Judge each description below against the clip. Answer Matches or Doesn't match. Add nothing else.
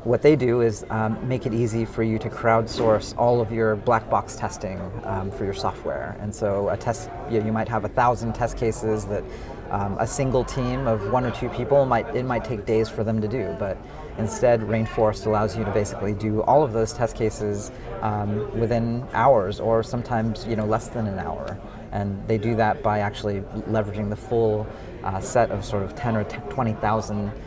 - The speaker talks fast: Matches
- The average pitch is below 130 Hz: Matches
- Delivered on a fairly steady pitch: Matches